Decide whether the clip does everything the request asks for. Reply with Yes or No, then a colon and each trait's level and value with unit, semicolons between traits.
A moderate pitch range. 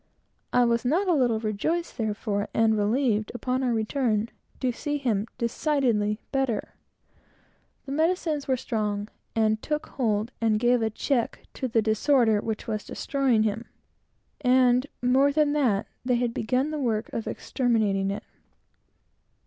Yes: average, 3.7 semitones